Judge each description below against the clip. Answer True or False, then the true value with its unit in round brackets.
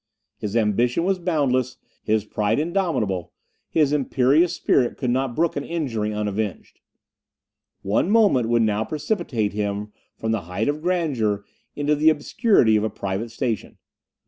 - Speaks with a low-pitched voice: True (120 Hz)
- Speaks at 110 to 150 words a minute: True (145 wpm)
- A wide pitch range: True (6.2 semitones)